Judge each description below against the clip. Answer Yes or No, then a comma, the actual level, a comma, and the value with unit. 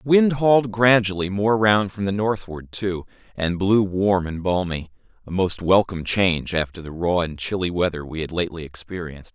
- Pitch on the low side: Yes, very low, 95 Hz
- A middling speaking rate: Yes, average, 185 wpm